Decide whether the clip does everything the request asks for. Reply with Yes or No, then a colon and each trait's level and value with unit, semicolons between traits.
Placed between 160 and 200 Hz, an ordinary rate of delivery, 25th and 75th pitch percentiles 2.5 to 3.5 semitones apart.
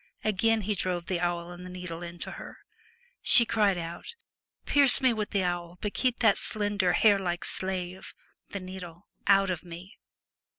Yes: medium, 185 Hz; average, 170 wpm; average, 2.9 semitones